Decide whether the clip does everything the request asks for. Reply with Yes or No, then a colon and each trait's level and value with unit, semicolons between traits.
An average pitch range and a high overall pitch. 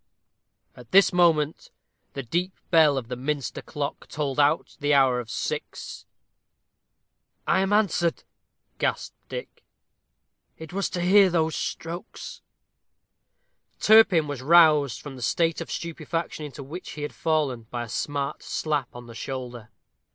No: average, 4.1 semitones; medium, 150 Hz